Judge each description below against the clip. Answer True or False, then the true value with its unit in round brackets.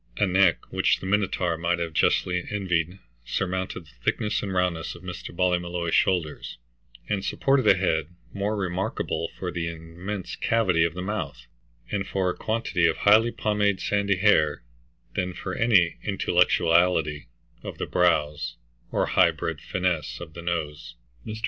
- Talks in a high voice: False (90 Hz)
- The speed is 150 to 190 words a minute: True (155 wpm)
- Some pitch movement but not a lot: True (3.0 semitones)